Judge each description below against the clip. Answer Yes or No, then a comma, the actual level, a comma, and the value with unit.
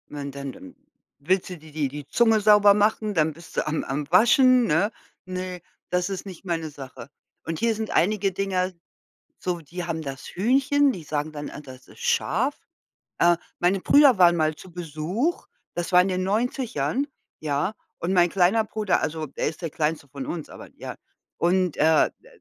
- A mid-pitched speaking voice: Yes, medium, 180 Hz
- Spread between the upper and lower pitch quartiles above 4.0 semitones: Yes, average, 5.2 semitones